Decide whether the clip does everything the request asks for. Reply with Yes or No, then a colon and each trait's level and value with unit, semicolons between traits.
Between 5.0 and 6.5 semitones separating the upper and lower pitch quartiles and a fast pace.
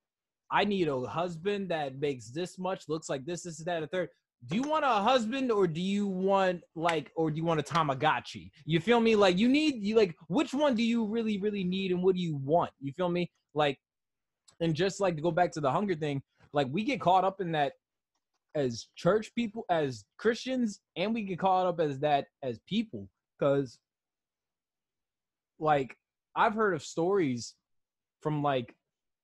No: wide, 5.6 semitones; average, 195 wpm